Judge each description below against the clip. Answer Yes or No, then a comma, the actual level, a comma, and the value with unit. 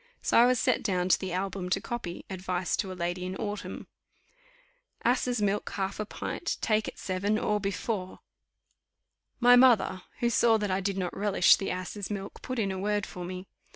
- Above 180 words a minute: Yes, average, 190 wpm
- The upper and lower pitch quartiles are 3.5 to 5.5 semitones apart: No, narrow, 2.6 semitones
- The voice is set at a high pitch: Yes, high, 195 Hz